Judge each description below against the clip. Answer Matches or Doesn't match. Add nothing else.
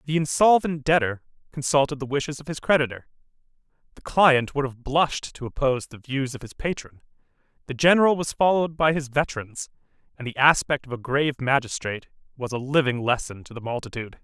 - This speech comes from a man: Matches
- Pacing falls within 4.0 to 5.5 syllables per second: Doesn't match